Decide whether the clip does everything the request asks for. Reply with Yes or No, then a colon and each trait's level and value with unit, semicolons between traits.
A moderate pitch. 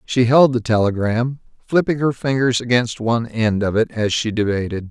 No: low, 120 Hz